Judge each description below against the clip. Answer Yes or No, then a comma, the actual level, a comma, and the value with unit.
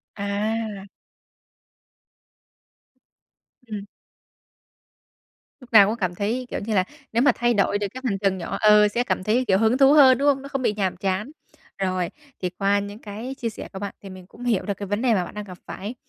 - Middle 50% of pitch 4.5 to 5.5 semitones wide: No, average, 3.4 semitones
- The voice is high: Yes, high, 210 Hz